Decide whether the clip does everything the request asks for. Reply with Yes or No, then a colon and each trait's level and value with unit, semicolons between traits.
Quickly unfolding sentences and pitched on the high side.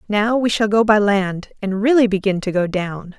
Yes: fast, 225 wpm; high, 205 Hz